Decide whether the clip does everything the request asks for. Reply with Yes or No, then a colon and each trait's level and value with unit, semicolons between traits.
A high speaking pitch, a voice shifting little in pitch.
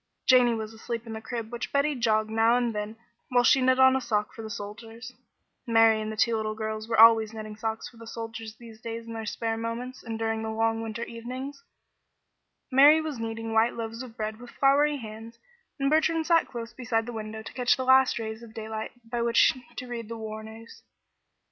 Yes: high, 230 Hz; narrow, 1.8 semitones